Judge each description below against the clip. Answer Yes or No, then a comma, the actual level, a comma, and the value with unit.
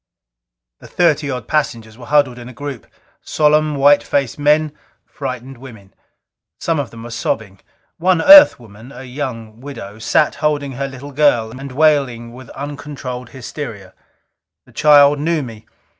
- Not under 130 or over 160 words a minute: Yes, average, 150 wpm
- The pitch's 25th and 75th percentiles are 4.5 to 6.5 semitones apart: No, average, 3.7 semitones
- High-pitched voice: No, low, 135 Hz